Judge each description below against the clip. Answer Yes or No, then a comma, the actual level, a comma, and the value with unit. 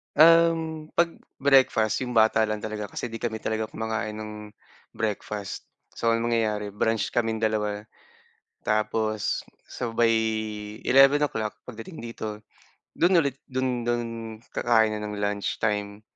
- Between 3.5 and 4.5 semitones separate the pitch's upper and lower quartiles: No, average, 2.9 semitones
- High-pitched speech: No, low, 110 Hz